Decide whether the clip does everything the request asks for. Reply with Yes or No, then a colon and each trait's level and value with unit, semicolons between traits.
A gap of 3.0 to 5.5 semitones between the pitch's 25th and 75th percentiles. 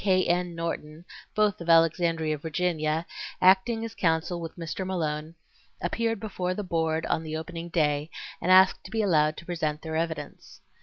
No: narrow, 2.6 semitones